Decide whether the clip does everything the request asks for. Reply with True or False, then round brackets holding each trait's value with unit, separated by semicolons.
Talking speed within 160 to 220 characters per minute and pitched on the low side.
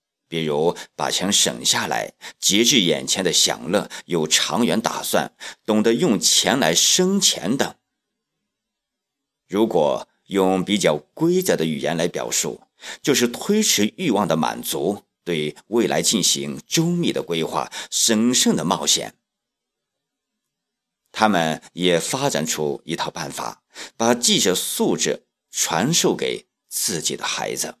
True (190 characters per minute; 120 Hz)